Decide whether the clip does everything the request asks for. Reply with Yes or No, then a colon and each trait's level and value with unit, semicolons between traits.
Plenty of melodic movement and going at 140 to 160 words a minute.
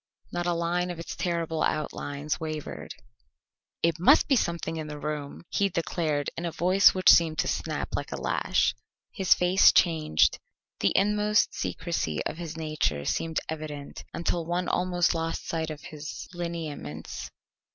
No: narrow, 2.4 semitones; average, 155 wpm